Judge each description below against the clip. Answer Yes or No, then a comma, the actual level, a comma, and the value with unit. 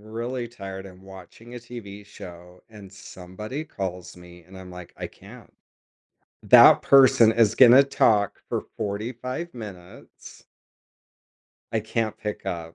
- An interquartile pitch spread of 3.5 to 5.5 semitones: Yes, average, 4.2 semitones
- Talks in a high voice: No, low, 105 Hz